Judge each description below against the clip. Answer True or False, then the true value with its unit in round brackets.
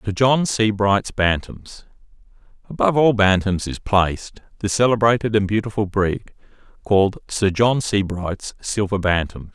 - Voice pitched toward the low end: True (105 Hz)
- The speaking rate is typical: False (120 wpm)